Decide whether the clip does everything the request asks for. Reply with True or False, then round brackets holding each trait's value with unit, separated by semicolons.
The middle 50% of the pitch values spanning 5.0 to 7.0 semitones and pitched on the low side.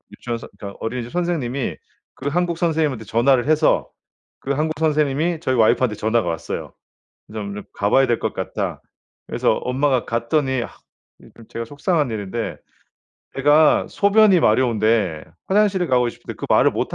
True (5.3 semitones; 130 Hz)